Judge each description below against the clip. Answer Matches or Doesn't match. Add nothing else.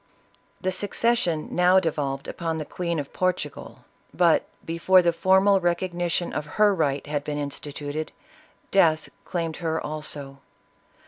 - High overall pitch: Doesn't match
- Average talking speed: Doesn't match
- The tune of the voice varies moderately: Matches